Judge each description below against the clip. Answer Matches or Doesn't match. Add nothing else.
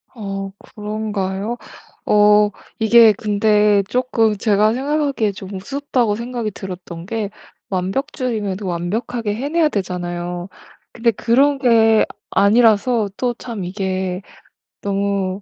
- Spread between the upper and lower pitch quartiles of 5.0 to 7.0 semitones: Doesn't match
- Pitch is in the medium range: Doesn't match